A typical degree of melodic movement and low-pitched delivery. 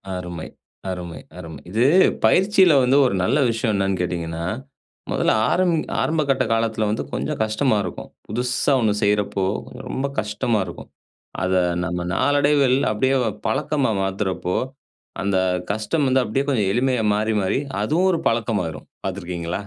No: wide, 6.0 semitones; low, 110 Hz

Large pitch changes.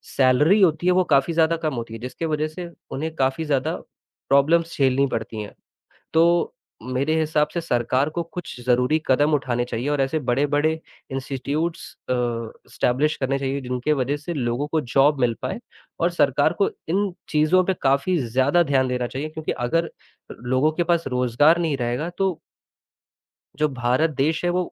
No: average, 3.9 semitones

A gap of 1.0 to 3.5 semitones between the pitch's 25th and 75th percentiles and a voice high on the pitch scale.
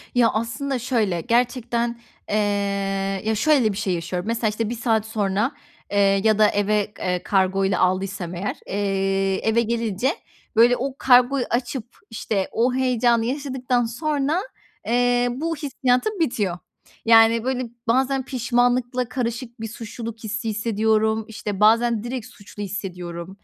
Yes: average, 3.2 semitones; high, 230 Hz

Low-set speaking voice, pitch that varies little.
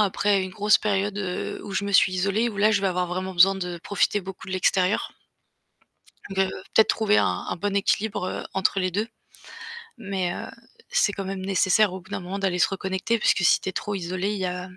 No: high, 195 Hz; narrow, 1.7 semitones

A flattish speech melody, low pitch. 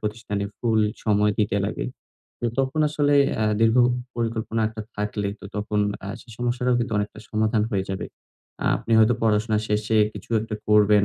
Yes: narrow, 1.8 semitones; low, 110 Hz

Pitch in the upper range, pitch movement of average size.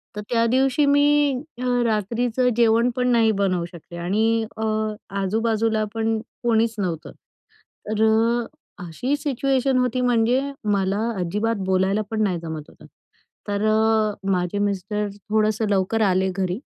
Yes: high, 220 Hz; average, 3.5 semitones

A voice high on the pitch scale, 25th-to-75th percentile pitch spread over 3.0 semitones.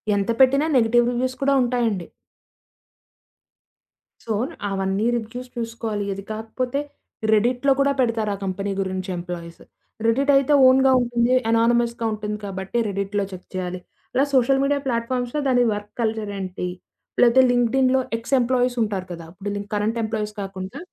Yes: high, 230 Hz; average, 3.8 semitones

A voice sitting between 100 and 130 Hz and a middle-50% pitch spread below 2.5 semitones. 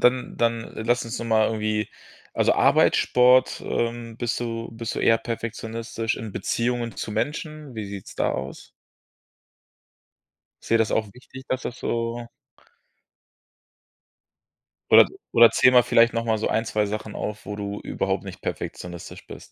Yes: low, 115 Hz; narrow, 1.6 semitones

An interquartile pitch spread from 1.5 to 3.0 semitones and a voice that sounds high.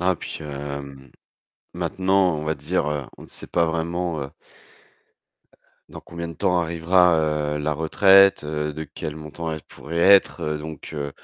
No: narrow, 2.6 semitones; very low, 80 Hz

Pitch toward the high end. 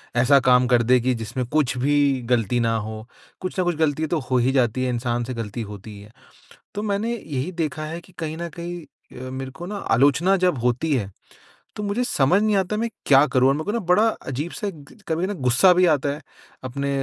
No: medium, 140 Hz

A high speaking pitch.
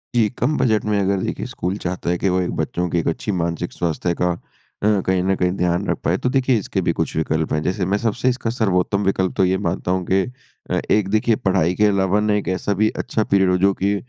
No: very low, 95 Hz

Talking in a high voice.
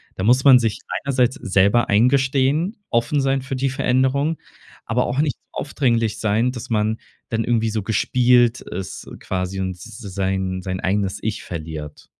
No: low, 115 Hz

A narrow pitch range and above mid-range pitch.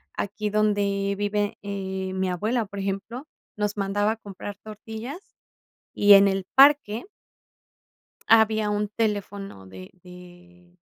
Yes: narrow, 1.8 semitones; high, 205 Hz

